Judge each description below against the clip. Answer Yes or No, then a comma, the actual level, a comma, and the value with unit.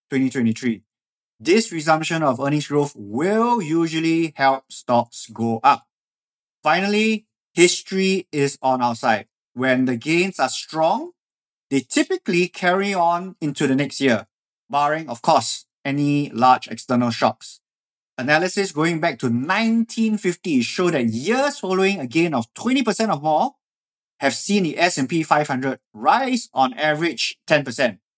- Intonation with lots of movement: Yes, wide, 6.2 semitones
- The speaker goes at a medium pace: No, slow, 130 wpm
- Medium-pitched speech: Yes, medium, 155 Hz